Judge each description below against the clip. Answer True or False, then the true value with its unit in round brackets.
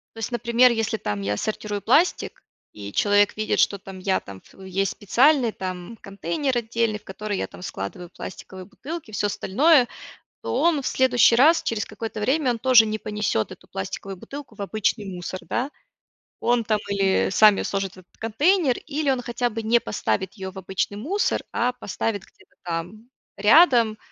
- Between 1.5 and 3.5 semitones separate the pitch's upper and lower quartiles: False (4.2 semitones)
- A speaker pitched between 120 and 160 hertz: False (215 Hz)